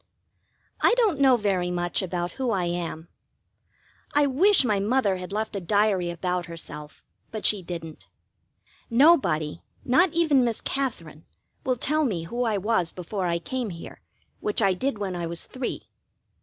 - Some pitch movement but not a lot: No, wide, 6.9 semitones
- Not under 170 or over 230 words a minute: No, average, 160 wpm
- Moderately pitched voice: No, high, 200 Hz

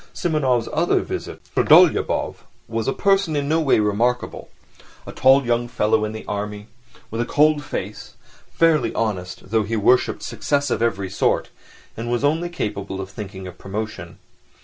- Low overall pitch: Yes, low, 115 Hz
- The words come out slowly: No, average, 155 wpm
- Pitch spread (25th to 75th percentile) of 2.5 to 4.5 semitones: No, wide, 5.4 semitones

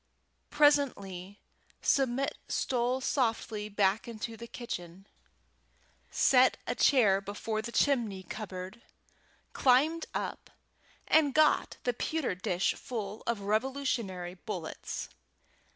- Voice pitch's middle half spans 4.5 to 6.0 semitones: Yes, average, 5.0 semitones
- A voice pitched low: No, high, 225 Hz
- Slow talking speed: Yes, slow, 100 wpm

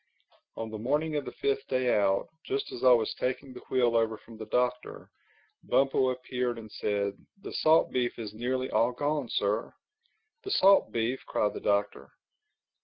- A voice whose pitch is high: No, low, 125 Hz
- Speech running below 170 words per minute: No, average, 175 wpm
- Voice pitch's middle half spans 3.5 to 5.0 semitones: No, average, 3.0 semitones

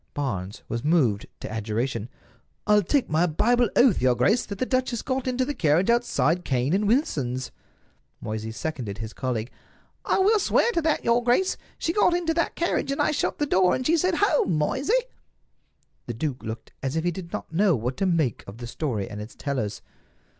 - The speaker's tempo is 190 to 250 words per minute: Yes, average, 195 wpm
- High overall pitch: No, medium, 170 Hz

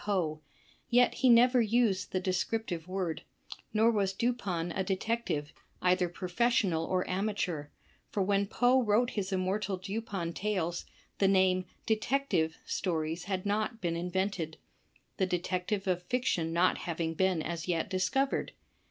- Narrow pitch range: No, average, 3.5 semitones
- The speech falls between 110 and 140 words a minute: Yes, slow, 135 wpm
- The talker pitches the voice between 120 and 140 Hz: No, high, 190 Hz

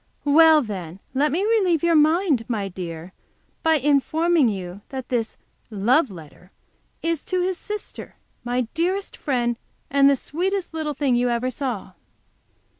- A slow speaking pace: No, average, 145 wpm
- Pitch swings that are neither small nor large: No, wide, 6.2 semitones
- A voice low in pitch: No, very high, 280 Hz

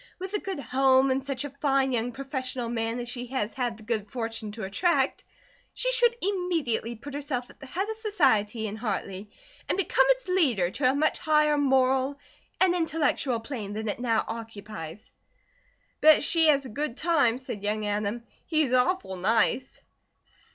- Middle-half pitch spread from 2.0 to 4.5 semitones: No, average, 5.1 semitones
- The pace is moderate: Yes, average, 175 wpm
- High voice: Yes, very high, 260 Hz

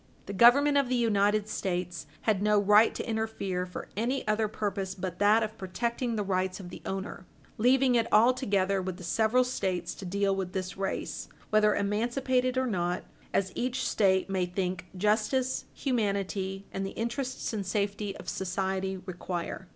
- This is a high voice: Yes, high, 200 Hz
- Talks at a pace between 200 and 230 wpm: No, average, 165 wpm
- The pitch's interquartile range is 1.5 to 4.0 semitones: Yes, average, 3.3 semitones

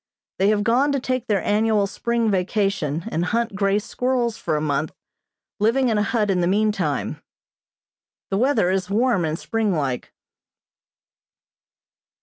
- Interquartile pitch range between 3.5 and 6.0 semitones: Yes, average, 4.0 semitones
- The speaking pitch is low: No, high, 210 Hz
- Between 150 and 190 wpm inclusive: No, average, 140 wpm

